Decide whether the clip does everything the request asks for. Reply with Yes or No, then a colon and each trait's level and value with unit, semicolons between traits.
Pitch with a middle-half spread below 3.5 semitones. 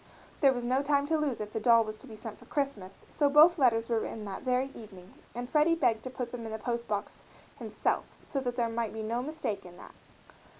No: average, 3.8 semitones